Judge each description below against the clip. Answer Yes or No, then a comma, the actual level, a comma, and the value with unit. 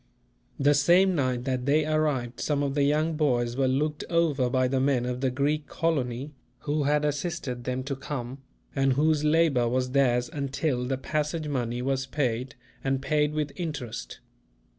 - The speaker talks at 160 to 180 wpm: Yes, average, 170 wpm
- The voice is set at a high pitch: No, medium, 140 Hz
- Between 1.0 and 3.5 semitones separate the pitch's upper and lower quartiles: Yes, average, 2.9 semitones